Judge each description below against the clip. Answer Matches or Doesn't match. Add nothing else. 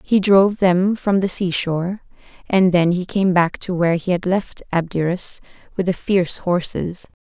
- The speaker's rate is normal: Matches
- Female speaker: Matches